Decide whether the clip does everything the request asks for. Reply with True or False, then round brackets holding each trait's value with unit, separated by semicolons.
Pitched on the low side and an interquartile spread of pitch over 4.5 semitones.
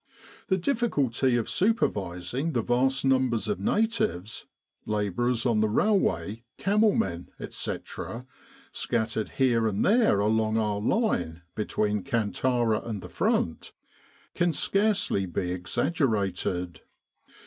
True (115 Hz; 5.1 semitones)